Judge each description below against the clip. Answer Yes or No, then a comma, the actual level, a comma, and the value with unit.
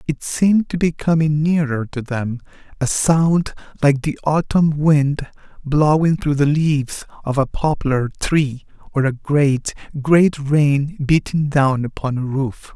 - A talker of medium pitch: Yes, medium, 145 Hz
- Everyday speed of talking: Yes, average, 145 wpm